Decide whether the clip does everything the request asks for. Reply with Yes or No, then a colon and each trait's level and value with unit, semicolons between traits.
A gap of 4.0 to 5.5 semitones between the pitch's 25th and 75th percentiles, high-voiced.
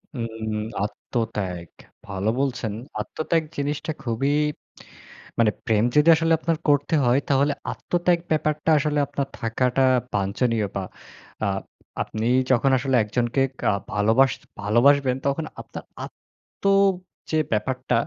No: average, 4.6 semitones; low, 130 Hz